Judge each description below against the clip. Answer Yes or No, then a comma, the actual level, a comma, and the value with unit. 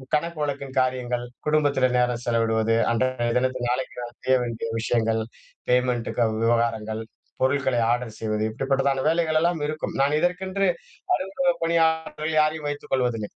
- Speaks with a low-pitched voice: Yes, low, 130 Hz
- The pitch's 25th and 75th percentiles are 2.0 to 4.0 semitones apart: No, average, 4.5 semitones